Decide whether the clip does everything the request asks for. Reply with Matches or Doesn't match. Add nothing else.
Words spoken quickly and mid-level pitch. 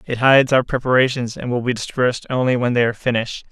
Doesn't match